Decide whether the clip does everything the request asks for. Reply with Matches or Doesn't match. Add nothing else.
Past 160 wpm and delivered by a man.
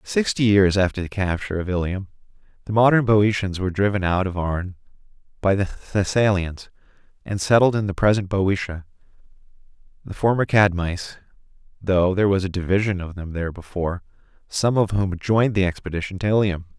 Doesn't match